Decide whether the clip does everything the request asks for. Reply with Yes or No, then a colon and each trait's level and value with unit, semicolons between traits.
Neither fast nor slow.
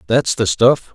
Yes: average, 190 wpm